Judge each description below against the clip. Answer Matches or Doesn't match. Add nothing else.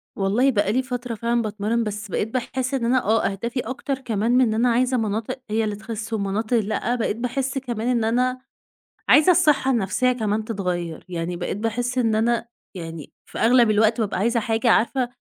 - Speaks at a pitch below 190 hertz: Doesn't match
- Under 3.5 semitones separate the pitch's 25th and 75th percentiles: Matches